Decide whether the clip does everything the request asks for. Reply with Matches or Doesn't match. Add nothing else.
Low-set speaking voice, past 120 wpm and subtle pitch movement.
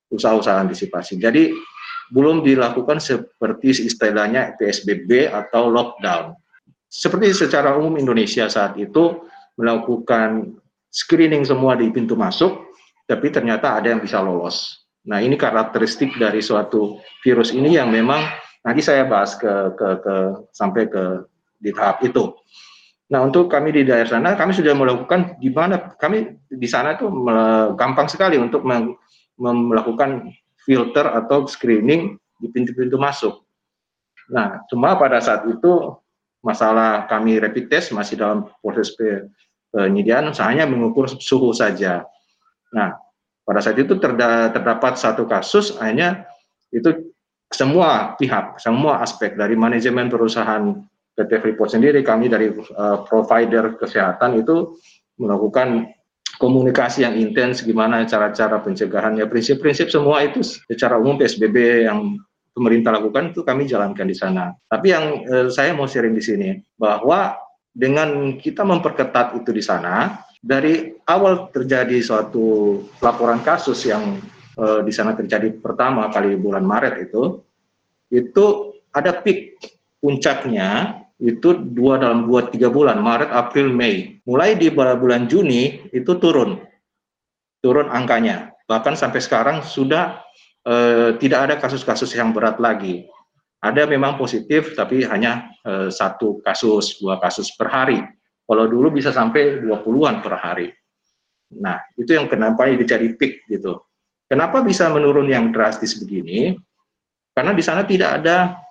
Doesn't match